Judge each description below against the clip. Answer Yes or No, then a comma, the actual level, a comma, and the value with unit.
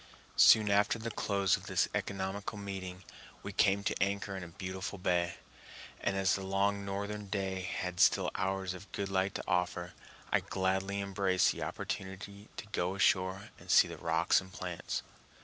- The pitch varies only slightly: Yes, narrow, 1.3 semitones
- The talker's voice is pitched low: Yes, very low, 95 Hz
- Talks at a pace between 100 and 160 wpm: No, average, 170 wpm